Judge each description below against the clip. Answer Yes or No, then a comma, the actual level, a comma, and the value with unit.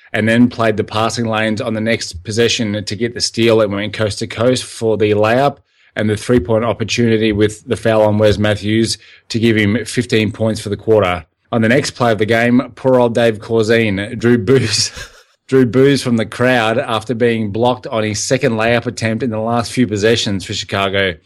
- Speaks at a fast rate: Yes, fast, 210 wpm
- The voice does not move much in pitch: Yes, narrow, 1.8 semitones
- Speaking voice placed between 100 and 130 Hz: Yes, low, 110 Hz